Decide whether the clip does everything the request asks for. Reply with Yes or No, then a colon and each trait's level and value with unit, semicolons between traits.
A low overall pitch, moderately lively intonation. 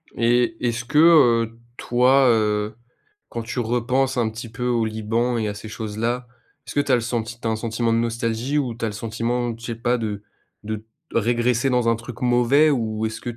No: low, 115 Hz; narrow, 1.7 semitones